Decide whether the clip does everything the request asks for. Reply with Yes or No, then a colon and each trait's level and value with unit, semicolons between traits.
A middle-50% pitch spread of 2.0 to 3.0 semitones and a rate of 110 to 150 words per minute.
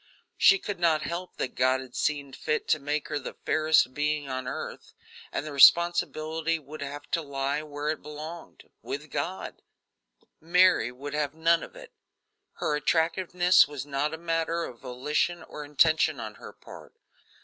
No: average, 2.7 semitones; average, 165 wpm